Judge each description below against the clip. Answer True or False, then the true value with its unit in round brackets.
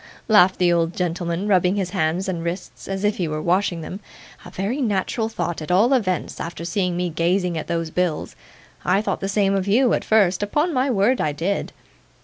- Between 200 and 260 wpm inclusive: True (205 wpm)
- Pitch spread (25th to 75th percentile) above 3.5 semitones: False (3.1 semitones)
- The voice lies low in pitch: False (185 Hz)